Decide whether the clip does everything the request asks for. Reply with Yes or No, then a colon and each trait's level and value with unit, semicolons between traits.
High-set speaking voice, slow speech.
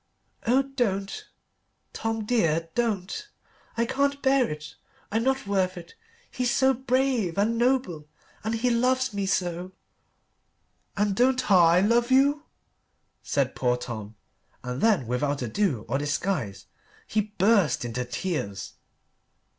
Yes: high, 200 Hz; slow, 125 wpm